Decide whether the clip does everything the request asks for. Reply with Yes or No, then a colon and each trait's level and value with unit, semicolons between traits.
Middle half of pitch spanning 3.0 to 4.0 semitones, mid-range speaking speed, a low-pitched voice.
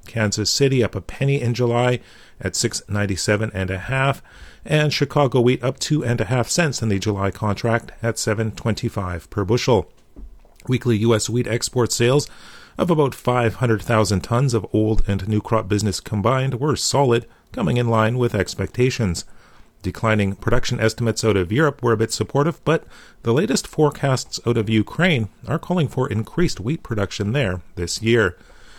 Yes: average, 3.3 semitones; average, 175 wpm; low, 115 Hz